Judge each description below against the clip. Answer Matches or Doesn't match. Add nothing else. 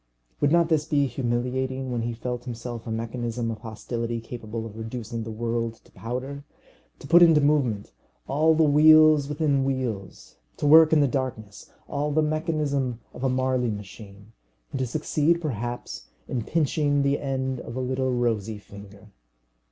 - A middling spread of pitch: Matches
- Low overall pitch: Matches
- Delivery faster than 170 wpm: Doesn't match